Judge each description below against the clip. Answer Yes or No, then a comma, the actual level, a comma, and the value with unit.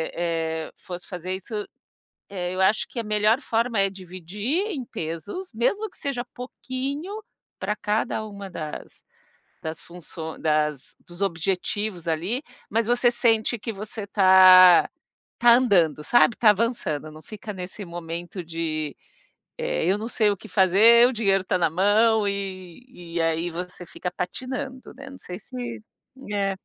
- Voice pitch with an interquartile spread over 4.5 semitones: Yes, average, 4.9 semitones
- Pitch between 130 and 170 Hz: No, high, 195 Hz